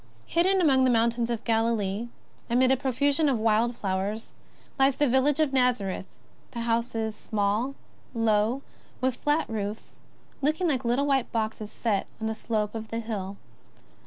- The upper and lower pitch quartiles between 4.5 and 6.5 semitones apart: No, average, 3.4 semitones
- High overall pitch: Yes, high, 235 Hz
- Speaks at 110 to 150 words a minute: No, average, 160 wpm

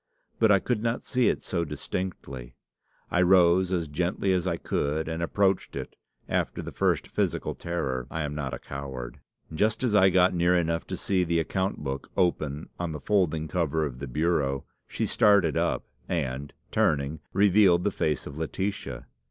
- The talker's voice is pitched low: Yes, very low, 85 Hz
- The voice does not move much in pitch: No, average, 4.2 semitones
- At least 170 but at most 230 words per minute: Yes, average, 175 wpm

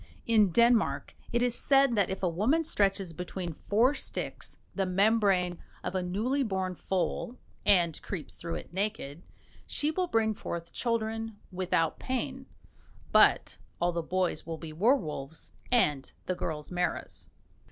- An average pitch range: Yes, average, 5.0 semitones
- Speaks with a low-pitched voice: No, high, 195 Hz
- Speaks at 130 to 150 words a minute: Yes, average, 145 wpm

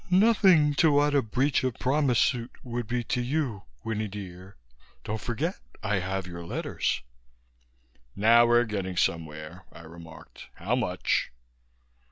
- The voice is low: Yes, low, 115 Hz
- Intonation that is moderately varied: No, wide, 6.0 semitones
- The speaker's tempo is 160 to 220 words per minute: No, average, 140 wpm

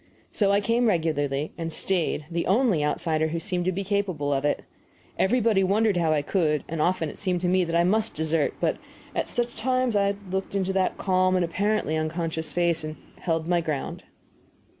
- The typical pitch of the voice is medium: Yes, medium, 175 Hz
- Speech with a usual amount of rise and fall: Yes, average, 3.9 semitones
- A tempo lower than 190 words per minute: No, average, 195 wpm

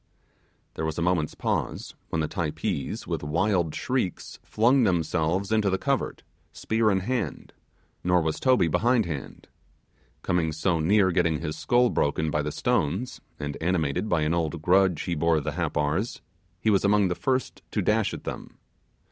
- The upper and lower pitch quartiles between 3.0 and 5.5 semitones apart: Yes, average, 4.6 semitones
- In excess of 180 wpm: No, average, 165 wpm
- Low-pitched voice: Yes, very low, 90 Hz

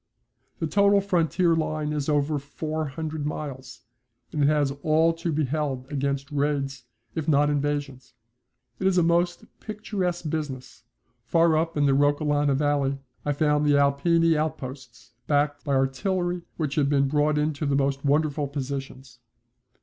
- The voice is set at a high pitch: No, medium, 145 Hz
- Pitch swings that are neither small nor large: No, narrow, 2.3 semitones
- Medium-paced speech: Yes, average, 150 wpm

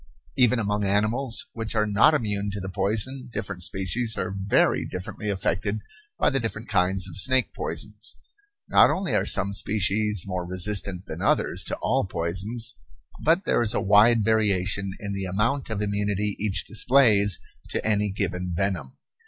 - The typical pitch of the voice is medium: No, low, 105 Hz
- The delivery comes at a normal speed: Yes, average, 160 wpm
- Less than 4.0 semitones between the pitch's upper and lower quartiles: Yes, narrow, 2.5 semitones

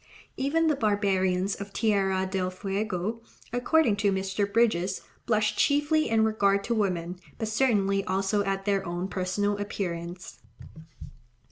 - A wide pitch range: No, narrow, 2.5 semitones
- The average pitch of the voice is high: Yes, high, 200 Hz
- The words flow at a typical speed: No, slow, 130 wpm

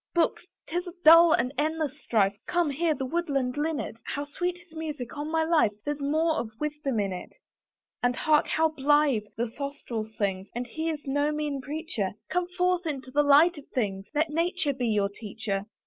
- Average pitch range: Yes, average, 4.7 semitones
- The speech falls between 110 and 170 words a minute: No, average, 190 wpm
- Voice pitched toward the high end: Yes, very high, 290 Hz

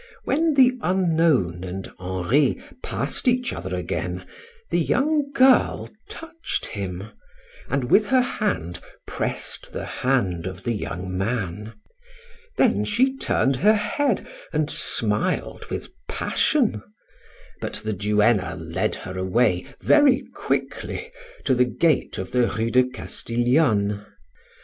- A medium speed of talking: No, slow, 120 wpm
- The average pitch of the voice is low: Yes, low, 125 Hz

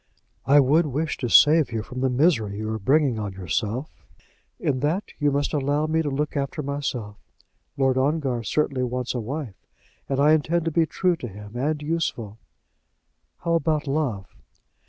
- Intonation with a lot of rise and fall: No, average, 4.2 semitones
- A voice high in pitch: No, medium, 140 Hz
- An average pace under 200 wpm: Yes, average, 175 wpm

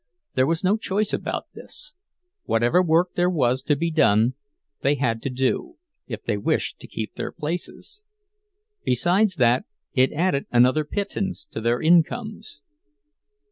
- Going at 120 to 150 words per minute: Yes, average, 140 wpm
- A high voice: No, medium, 155 Hz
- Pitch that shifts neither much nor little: No, wide, 7.3 semitones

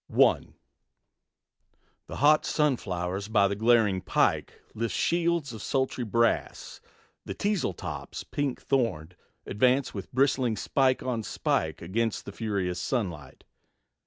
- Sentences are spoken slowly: Yes, slow, 120 wpm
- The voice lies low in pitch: Yes, low, 115 Hz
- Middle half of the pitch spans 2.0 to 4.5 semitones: No, average, 5.3 semitones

